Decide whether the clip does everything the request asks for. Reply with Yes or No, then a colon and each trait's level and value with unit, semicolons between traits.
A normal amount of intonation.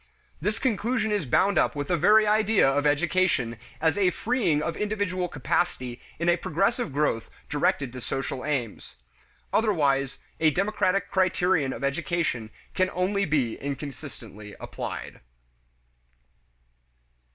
No: wide, 6.3 semitones